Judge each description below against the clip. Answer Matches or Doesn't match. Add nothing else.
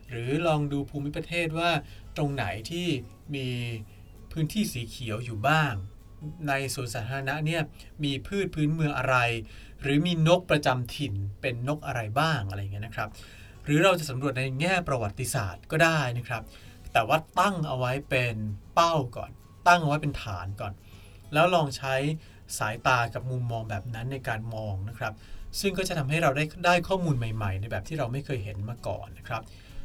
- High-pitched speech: Doesn't match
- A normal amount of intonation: Doesn't match